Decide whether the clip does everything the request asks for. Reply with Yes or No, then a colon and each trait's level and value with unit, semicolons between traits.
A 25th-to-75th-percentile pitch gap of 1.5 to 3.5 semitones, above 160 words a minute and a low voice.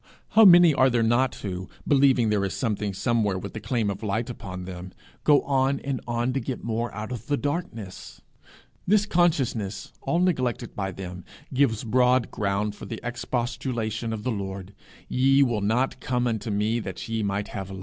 No: average, 4.1 semitones; average, 185 wpm; low, 115 Hz